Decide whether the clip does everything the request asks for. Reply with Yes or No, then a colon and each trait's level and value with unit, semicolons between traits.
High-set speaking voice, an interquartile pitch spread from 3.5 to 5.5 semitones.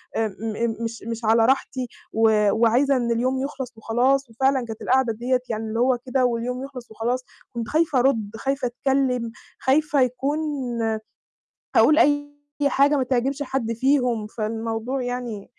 No: high, 245 Hz; average, 2.9 semitones